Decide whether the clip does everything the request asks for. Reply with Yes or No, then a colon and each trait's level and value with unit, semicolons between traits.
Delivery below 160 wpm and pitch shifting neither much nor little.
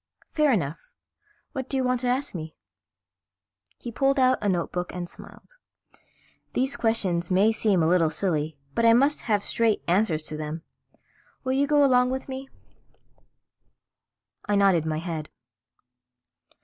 No: average, 150 wpm; wide, 7.3 semitones